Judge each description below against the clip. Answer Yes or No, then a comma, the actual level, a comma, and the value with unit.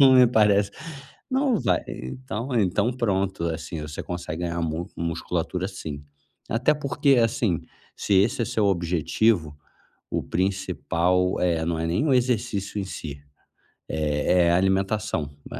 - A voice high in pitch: No, very low, 95 Hz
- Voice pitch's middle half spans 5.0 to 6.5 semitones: Yes, average, 5.3 semitones